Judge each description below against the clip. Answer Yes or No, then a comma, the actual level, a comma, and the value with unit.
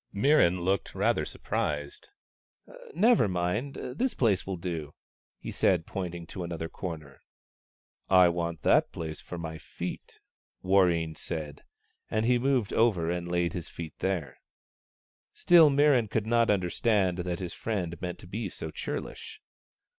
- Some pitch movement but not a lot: Yes, average, 4.8 semitones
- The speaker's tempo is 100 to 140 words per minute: No, average, 150 wpm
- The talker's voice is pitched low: Yes, very low, 90 Hz